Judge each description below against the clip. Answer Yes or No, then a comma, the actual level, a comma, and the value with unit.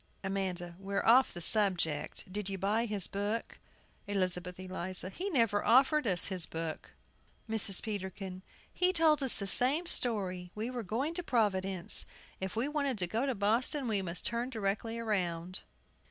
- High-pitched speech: Yes, high, 205 Hz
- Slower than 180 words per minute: Yes, average, 160 wpm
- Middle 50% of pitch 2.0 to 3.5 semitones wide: No, average, 4.3 semitones